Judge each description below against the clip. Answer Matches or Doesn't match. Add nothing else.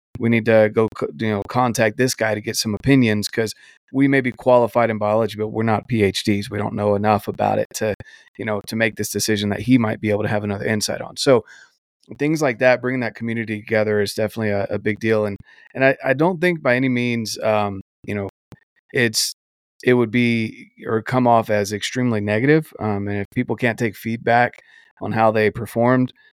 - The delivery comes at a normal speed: Doesn't match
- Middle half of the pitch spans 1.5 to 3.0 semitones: Matches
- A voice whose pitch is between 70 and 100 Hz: Doesn't match